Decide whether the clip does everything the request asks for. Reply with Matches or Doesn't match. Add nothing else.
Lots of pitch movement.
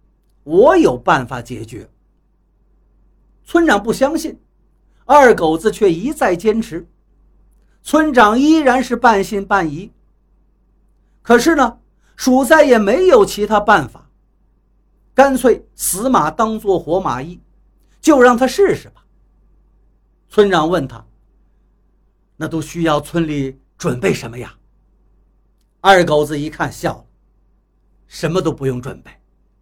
Matches